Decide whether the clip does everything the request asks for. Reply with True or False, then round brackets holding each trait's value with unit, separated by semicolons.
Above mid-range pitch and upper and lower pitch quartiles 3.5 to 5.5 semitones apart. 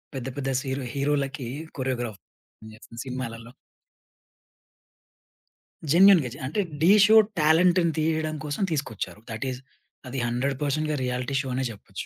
False (135 Hz; 3.8 semitones)